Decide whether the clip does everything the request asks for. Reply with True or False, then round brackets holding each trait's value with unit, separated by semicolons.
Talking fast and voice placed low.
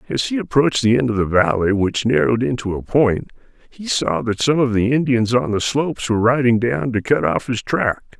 True (225 wpm; 120 Hz)